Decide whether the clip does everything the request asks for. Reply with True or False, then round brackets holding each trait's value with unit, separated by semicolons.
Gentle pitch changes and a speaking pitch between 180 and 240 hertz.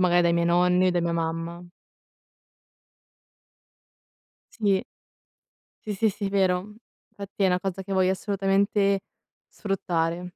True (2.1 semitones; 185 Hz)